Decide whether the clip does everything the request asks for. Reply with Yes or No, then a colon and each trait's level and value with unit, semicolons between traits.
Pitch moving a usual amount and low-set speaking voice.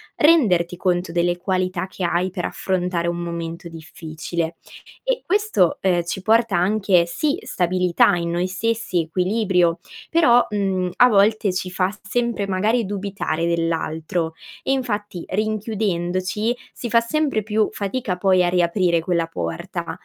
No: average, 3.8 semitones; medium, 185 Hz